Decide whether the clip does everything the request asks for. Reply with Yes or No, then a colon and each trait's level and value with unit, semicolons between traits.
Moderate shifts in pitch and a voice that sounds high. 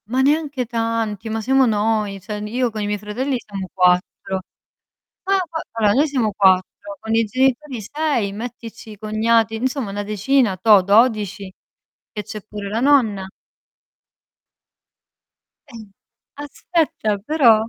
Yes: average, 3.9 semitones; high, 220 Hz